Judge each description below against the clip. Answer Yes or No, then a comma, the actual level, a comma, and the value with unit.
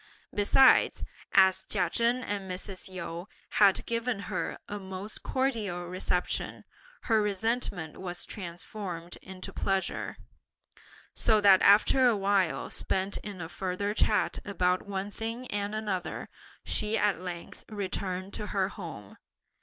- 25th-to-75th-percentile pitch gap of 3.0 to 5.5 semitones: No, narrow, 2.4 semitones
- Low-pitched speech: No, high, 195 Hz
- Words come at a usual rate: No, slow, 130 wpm